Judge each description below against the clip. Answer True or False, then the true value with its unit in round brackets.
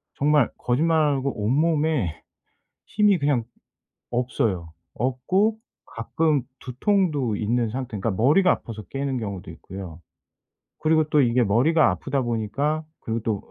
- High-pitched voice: False (130 Hz)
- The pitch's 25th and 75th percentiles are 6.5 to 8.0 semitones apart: False (5.4 semitones)